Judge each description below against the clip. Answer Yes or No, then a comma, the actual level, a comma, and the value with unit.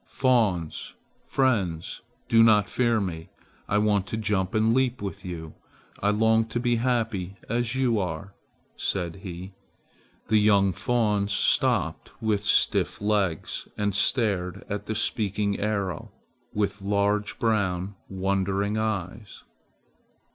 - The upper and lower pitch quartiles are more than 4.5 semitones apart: No, narrow, 2.6 semitones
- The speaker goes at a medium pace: No, slow, 125 wpm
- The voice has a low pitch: Yes, low, 105 Hz